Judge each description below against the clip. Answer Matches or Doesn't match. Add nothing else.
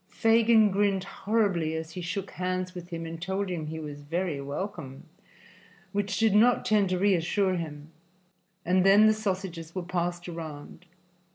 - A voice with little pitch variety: Doesn't match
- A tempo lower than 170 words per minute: Matches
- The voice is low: Doesn't match